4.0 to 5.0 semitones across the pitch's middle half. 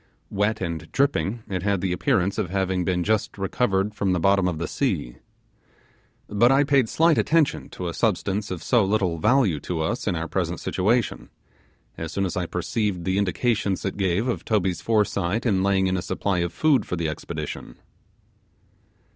No: average, 3.4 semitones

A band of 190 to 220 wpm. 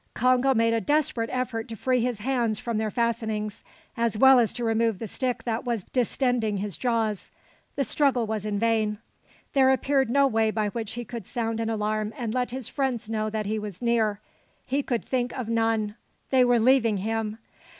Yes: average, 195 wpm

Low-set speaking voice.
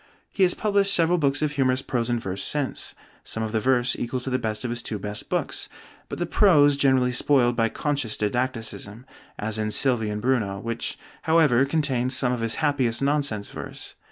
Yes: low, 125 Hz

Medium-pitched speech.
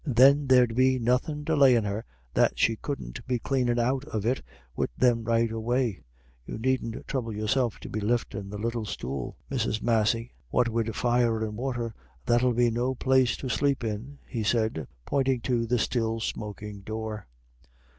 No: low, 115 Hz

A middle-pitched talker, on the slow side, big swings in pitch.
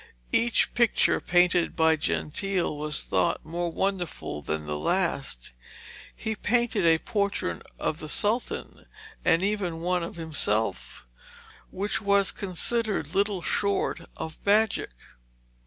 No: medium, 180 Hz; slow, 120 wpm; average, 4.0 semitones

